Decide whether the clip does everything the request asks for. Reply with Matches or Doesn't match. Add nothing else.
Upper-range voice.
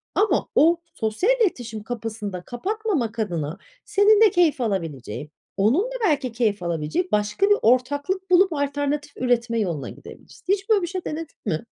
Matches